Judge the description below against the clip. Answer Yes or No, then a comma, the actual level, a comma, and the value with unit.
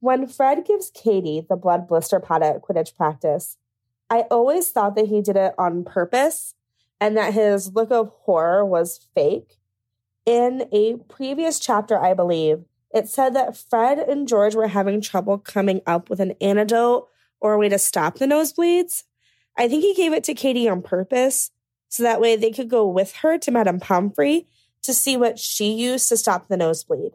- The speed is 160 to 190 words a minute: Yes, average, 185 wpm